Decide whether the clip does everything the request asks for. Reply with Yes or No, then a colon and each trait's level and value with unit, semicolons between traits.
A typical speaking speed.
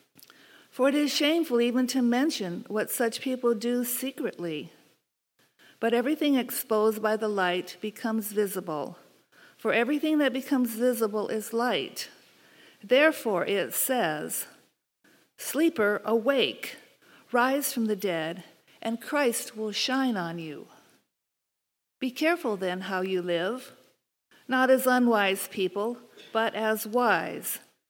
No: slow, 120 wpm